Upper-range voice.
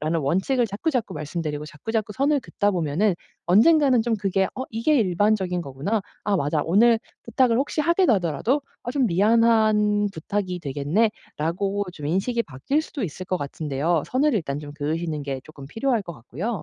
Yes: high, 195 Hz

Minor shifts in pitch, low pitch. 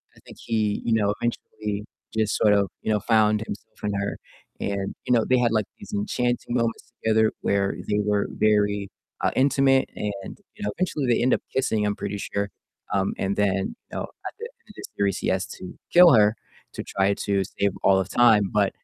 Yes: narrow, 2.3 semitones; low, 105 Hz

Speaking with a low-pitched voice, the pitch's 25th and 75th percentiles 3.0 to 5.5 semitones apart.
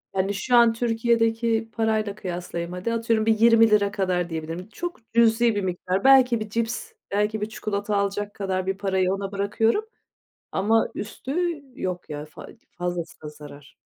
No: high, 205 Hz; average, 3.4 semitones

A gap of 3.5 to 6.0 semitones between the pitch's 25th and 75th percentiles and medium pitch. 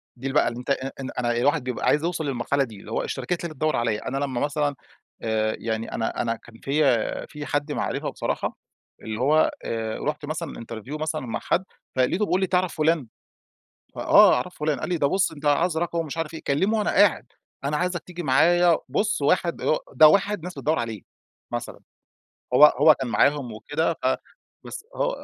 Yes: average, 5.0 semitones; medium, 145 Hz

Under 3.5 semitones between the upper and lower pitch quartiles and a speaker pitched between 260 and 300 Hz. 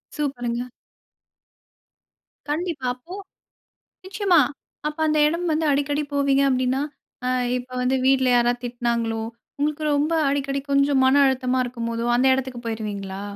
Yes: average, 3.1 semitones; very high, 265 Hz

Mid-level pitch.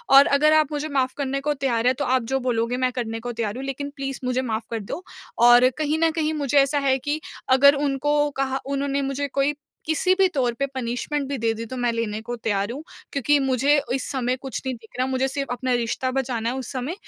No: very high, 265 Hz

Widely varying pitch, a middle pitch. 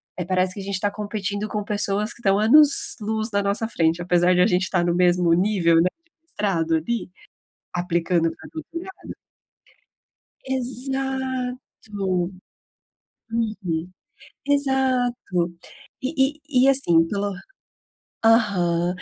No: wide, 5.8 semitones; high, 205 Hz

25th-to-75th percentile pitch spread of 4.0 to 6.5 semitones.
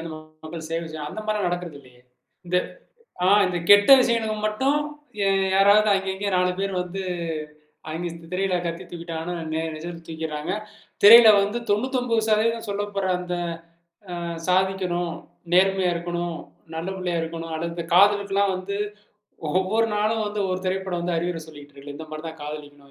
No: average, 3.6 semitones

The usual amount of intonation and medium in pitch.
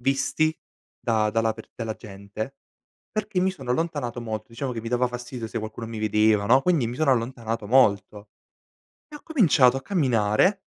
No: average, 3.9 semitones; low, 120 Hz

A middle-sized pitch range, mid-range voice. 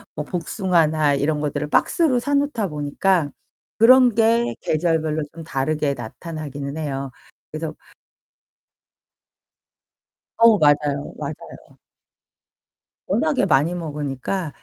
Yes: average, 4.7 semitones; medium, 155 Hz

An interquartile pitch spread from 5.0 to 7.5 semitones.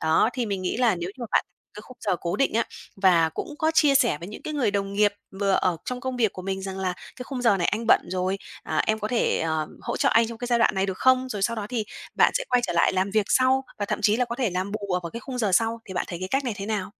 No: average, 4.5 semitones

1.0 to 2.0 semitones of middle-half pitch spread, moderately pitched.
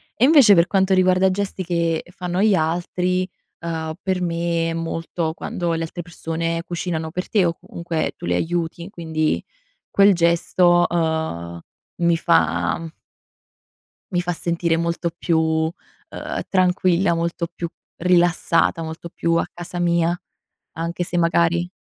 Yes: narrow, 1.3 semitones; medium, 170 Hz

